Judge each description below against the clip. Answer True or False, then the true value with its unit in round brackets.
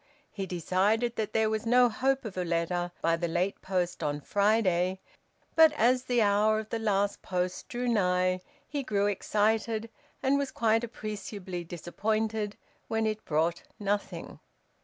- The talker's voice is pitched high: True (210 Hz)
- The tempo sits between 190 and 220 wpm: False (155 wpm)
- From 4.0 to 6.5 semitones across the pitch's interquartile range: False (3.6 semitones)